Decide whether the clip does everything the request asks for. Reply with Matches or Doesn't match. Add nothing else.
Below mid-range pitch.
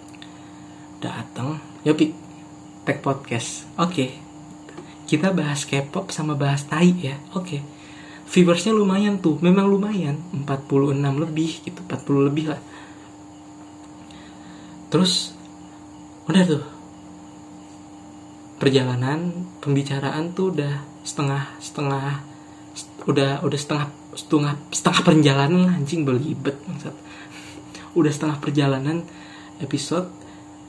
Doesn't match